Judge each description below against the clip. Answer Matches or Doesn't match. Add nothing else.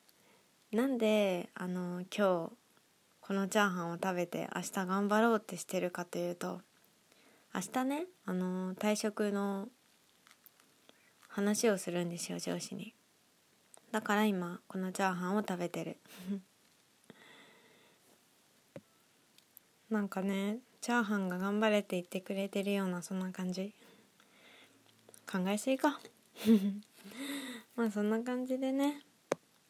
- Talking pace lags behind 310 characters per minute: Matches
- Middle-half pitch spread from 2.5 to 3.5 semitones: Matches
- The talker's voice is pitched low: Doesn't match